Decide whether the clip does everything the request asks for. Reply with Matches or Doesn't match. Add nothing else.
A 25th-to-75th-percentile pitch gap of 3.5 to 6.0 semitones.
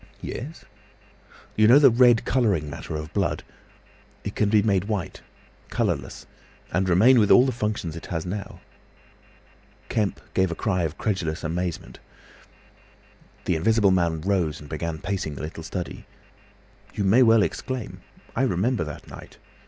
Matches